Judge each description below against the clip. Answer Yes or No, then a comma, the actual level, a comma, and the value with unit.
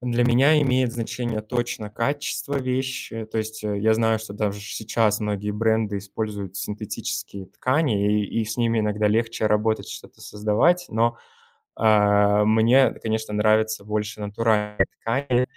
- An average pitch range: No, narrow, 2.0 semitones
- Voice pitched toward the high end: No, low, 110 Hz